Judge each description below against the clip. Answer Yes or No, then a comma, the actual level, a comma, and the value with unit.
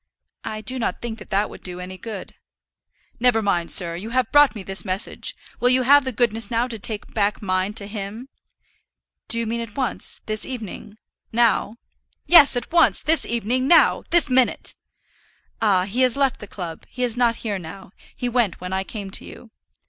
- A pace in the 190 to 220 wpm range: Yes, average, 195 wpm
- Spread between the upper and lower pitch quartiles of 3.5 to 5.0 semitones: Yes, average, 3.9 semitones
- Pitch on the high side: Yes, high, 225 Hz